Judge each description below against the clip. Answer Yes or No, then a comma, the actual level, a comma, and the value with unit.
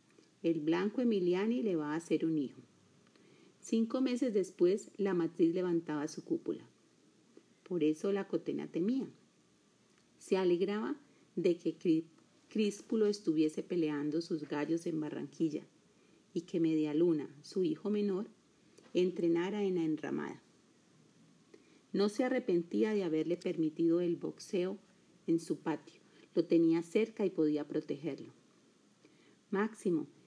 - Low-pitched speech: No, medium, 175 Hz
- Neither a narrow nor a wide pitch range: Yes, average, 3.9 semitones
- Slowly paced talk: Yes, slow, 120 wpm